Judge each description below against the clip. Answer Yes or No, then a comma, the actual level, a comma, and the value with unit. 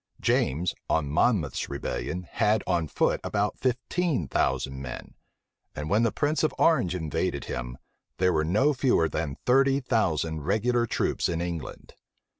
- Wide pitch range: Yes, wide, 7.9 semitones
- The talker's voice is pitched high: No, very low, 90 Hz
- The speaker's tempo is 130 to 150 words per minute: Yes, average, 145 wpm